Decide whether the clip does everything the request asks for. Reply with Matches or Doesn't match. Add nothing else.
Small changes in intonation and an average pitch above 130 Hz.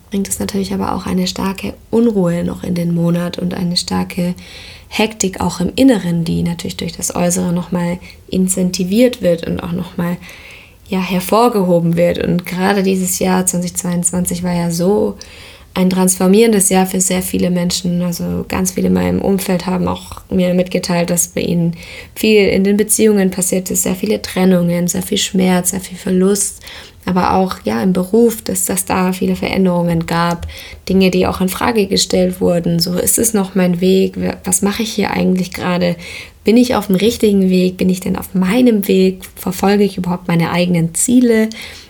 Matches